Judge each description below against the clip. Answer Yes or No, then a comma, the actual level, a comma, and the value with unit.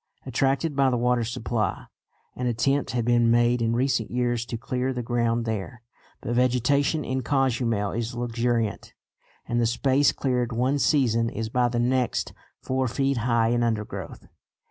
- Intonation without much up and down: Yes, narrow, 1.9 semitones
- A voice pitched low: Yes, low, 120 Hz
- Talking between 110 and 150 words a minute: No, average, 160 wpm